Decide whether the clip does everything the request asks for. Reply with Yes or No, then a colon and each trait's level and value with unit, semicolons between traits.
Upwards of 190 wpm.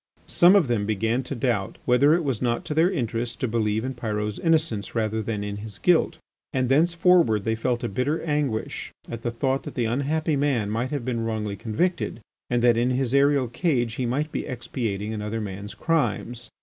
Yes: average, 200 wpm